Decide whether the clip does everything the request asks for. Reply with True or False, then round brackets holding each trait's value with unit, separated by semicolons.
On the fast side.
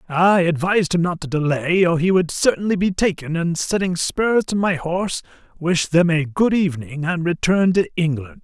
False (190 wpm)